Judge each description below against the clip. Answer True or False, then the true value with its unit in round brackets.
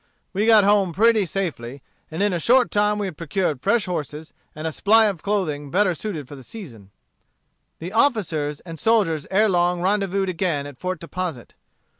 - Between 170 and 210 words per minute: True (180 wpm)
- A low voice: False (185 Hz)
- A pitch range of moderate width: True (5.0 semitones)